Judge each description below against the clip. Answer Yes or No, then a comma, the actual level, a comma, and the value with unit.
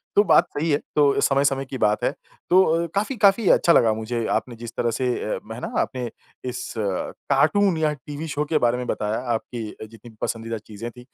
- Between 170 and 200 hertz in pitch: No, low, 130 Hz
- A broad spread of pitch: Yes, wide, 5.7 semitones